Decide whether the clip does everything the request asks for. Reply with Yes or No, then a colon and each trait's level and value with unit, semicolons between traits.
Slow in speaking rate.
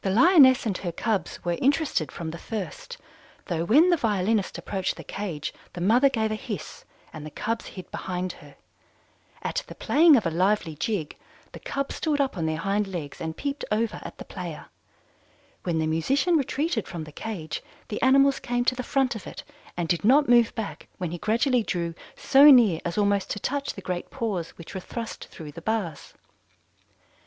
No: average, 195 wpm